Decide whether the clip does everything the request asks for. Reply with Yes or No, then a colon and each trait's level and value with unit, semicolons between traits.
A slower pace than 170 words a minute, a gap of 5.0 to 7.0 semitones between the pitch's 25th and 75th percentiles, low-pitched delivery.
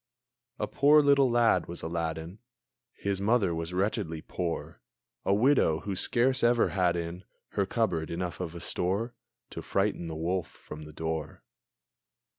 Yes: average, 150 wpm; average, 5.3 semitones; very low, 90 Hz